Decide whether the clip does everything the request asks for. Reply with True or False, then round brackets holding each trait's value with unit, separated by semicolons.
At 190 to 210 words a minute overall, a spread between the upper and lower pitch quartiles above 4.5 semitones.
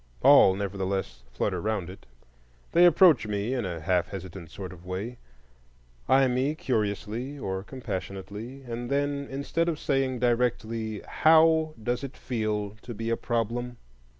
False (145 wpm; 5.2 semitones)